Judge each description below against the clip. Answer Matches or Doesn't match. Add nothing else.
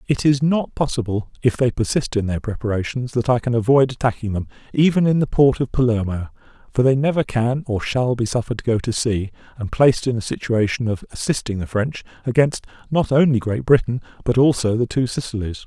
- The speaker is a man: Matches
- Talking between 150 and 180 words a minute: Doesn't match